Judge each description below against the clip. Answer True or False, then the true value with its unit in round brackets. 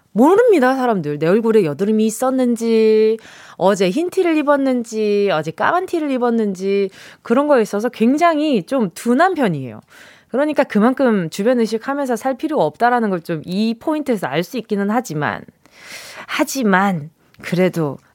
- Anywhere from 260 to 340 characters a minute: True (325 characters per minute)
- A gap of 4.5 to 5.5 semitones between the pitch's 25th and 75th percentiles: True (5.2 semitones)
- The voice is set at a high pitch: True (230 Hz)